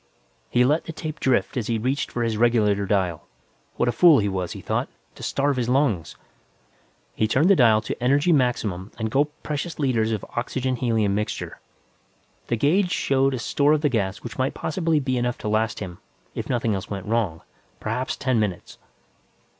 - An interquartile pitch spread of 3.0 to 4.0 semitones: No, average, 4.5 semitones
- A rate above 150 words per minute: Yes, average, 190 wpm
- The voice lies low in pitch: Yes, low, 120 Hz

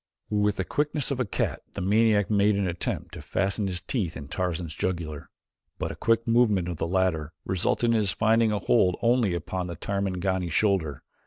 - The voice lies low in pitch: Yes, very low, 95 Hz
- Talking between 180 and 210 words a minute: Yes, average, 190 wpm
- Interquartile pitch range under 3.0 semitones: No, average, 3.6 semitones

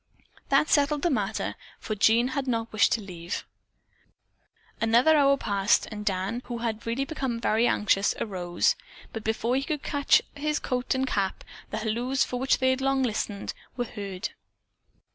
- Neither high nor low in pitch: No, high, 235 Hz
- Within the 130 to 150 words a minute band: No, average, 165 wpm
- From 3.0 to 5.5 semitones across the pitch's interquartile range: Yes, average, 4.2 semitones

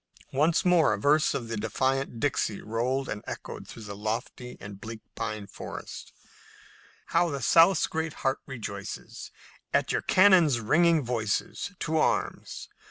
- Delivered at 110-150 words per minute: Yes, average, 145 wpm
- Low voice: Yes, low, 130 Hz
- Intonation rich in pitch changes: Yes, wide, 6.4 semitones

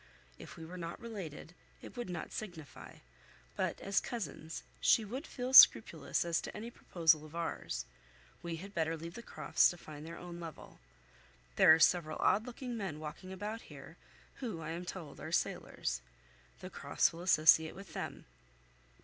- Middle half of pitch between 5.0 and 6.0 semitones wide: No, average, 4.2 semitones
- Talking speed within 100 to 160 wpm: No, average, 170 wpm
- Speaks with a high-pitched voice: No, medium, 170 Hz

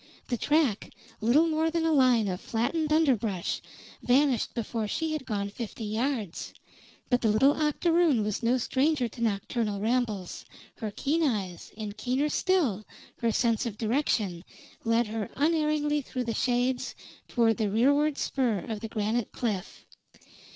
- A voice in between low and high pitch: No, high, 240 Hz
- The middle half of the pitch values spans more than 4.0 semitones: Yes, average, 5.2 semitones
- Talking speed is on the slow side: No, average, 150 wpm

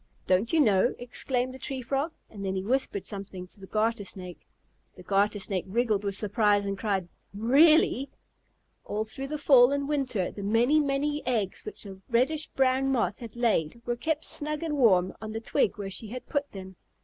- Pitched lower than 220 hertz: No, high, 230 Hz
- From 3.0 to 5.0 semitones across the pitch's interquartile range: No, wide, 5.4 semitones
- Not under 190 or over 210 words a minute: Yes, average, 195 wpm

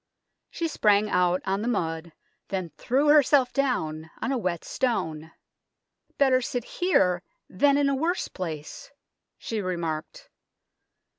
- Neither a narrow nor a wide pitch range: No, wide, 8.2 semitones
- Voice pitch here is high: Yes, high, 210 Hz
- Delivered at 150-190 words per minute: No, slow, 135 wpm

